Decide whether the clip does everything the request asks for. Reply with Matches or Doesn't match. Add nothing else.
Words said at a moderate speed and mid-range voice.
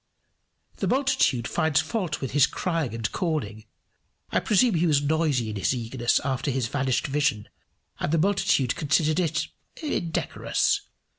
Matches